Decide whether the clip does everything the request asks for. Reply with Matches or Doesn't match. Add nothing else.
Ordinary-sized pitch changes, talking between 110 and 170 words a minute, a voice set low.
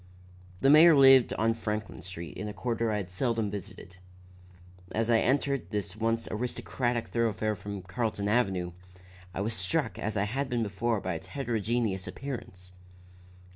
Matches